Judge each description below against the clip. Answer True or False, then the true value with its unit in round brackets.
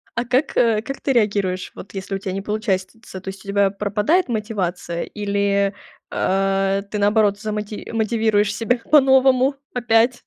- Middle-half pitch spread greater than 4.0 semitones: False (2.9 semitones)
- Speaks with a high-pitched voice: True (210 Hz)